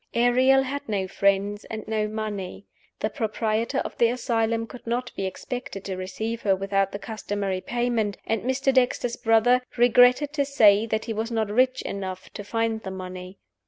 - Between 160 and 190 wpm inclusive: Yes, average, 175 wpm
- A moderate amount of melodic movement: Yes, average, 3.5 semitones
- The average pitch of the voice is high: Yes, high, 220 Hz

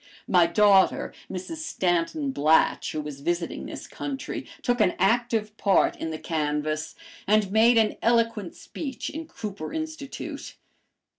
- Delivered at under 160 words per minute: Yes, slow, 135 wpm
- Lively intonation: Yes, wide, 6.4 semitones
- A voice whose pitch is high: Yes, high, 210 Hz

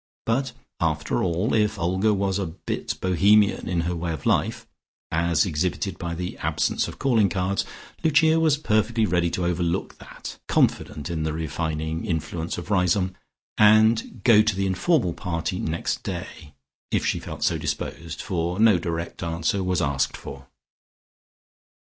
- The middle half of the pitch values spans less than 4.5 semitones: Yes, average, 4.1 semitones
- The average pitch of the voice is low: Yes, very low, 90 Hz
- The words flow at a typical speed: Yes, average, 155 wpm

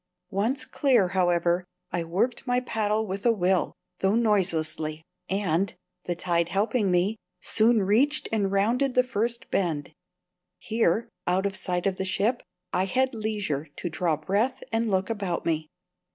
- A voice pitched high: Yes, high, 195 Hz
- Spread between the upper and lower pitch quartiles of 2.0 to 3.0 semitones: No, average, 4.4 semitones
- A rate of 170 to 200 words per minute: No, average, 150 wpm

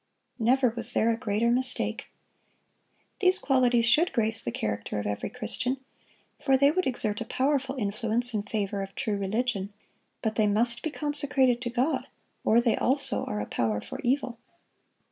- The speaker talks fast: No, average, 165 wpm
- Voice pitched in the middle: No, high, 235 Hz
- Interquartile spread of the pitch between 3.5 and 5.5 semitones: Yes, average, 3.8 semitones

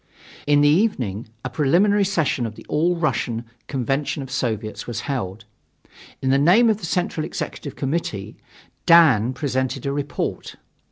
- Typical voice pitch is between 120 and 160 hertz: Yes, medium, 140 Hz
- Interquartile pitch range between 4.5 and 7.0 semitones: Yes, wide, 5.5 semitones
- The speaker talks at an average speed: Yes, average, 155 wpm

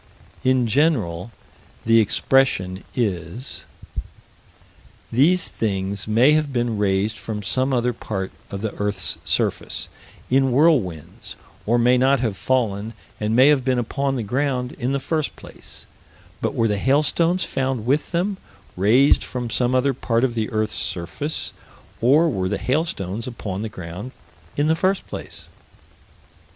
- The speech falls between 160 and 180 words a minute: No, average, 145 wpm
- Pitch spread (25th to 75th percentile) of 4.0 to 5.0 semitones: Yes, average, 4.6 semitones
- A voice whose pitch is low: Yes, low, 120 Hz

